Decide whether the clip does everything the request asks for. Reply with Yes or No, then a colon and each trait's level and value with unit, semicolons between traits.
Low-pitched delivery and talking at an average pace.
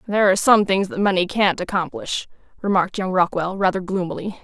No: high, 190 Hz; average, 175 wpm